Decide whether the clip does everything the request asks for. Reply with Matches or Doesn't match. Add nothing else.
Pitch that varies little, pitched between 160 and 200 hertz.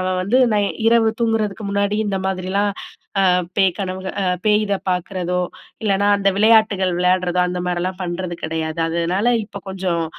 Matches